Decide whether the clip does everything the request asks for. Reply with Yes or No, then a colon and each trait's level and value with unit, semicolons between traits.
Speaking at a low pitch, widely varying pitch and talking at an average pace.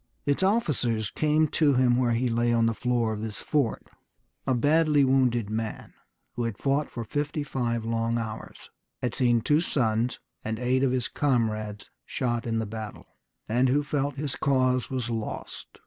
No: low, 125 Hz; average, 3.4 semitones; average, 180 wpm